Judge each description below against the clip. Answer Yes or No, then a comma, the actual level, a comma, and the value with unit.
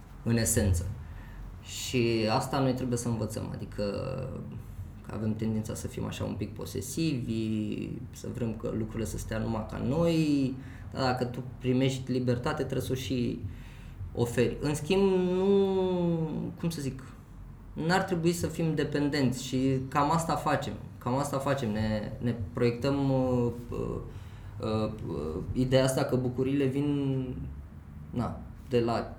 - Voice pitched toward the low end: Yes, low, 120 Hz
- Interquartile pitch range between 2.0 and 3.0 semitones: No, average, 3.7 semitones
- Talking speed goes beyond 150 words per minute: No, average, 140 wpm